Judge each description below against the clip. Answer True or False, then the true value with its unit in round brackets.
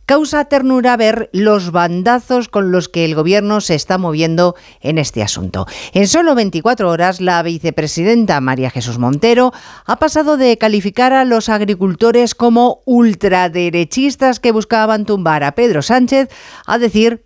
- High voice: True (210 Hz)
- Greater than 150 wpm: False (145 wpm)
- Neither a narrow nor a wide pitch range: False (5.8 semitones)